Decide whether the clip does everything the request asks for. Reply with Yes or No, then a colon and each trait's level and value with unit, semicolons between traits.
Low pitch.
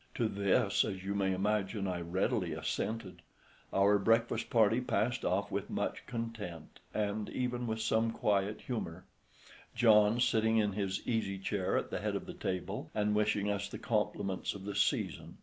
Yes: low, 105 Hz